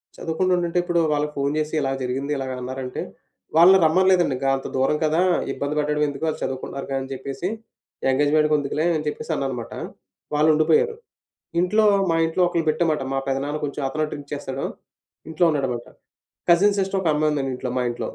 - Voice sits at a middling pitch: Yes, medium, 150 Hz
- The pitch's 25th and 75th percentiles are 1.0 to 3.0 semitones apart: No, average, 3.4 semitones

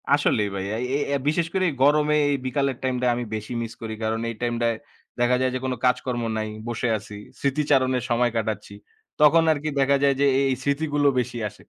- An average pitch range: Yes, average, 3.5 semitones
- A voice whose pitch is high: No, low, 125 Hz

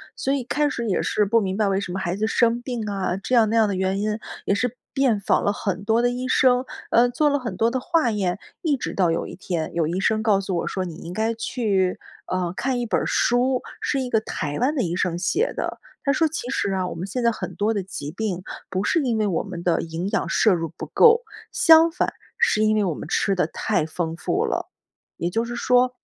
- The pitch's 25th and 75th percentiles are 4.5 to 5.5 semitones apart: Yes, average, 5.0 semitones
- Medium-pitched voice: No, high, 215 Hz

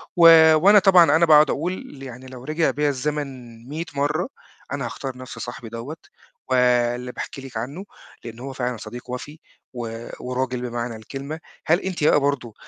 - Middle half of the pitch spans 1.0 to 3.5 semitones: No, average, 3.9 semitones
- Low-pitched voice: Yes, low, 130 Hz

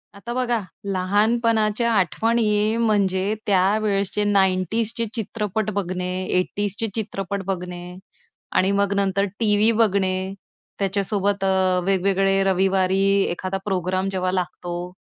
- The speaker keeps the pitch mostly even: Yes, narrow, 2.2 semitones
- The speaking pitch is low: No, high, 195 Hz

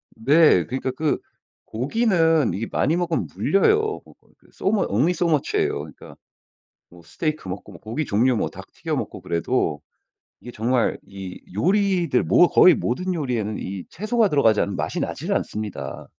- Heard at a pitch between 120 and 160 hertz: Yes, low, 135 Hz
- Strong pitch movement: Yes, wide, 8.8 semitones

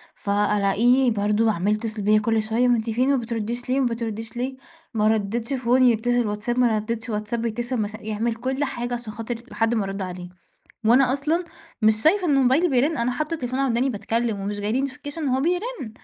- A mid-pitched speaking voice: No, high, 235 Hz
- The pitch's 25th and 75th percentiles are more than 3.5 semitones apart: No, average, 3.1 semitones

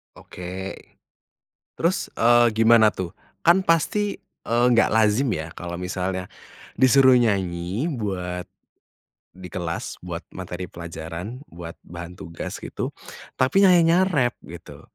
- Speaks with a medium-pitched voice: No, low, 100 Hz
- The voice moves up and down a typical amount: No, wide, 6.4 semitones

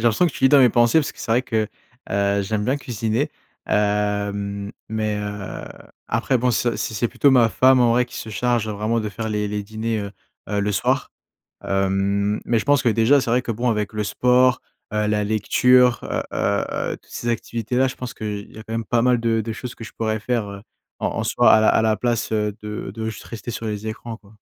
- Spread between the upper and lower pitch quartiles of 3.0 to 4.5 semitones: No, narrow, 2.5 semitones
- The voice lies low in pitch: Yes, low, 110 Hz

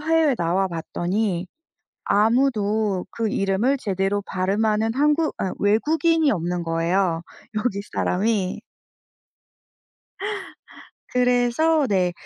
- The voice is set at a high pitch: Yes, high, 210 Hz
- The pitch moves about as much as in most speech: Yes, average, 5.0 semitones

